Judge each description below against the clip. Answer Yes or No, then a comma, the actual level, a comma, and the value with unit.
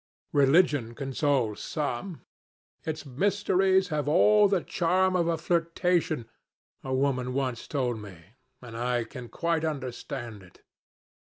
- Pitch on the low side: No, medium, 145 Hz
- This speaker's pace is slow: Yes, slow, 120 wpm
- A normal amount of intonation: No, wide, 5.8 semitones